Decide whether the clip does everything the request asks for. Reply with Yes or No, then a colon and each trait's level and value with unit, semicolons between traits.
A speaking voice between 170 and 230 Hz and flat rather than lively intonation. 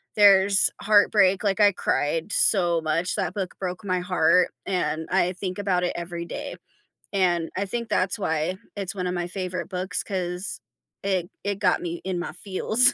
Yes: medium, 185 Hz; narrow, 2.1 semitones